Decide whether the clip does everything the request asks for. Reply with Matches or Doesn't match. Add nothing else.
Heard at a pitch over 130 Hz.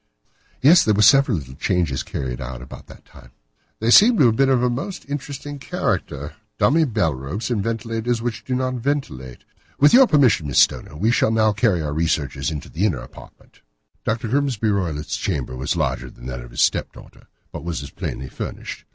Doesn't match